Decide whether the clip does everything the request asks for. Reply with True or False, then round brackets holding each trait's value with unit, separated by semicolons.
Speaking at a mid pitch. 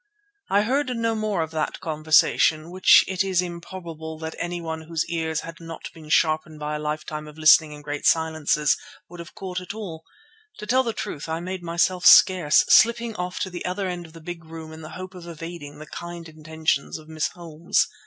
True (165 Hz)